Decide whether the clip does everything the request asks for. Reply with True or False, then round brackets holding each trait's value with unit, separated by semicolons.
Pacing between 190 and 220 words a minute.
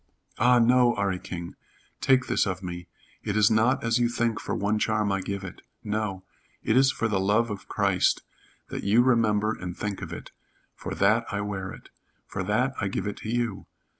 True (200 wpm)